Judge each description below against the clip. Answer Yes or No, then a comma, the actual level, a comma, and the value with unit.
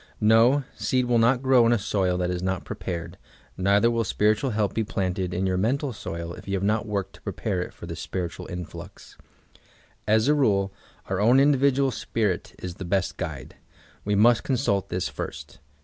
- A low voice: Yes, low, 105 Hz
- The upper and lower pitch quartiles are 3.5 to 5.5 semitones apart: Yes, average, 4.4 semitones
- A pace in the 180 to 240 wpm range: Yes, average, 190 wpm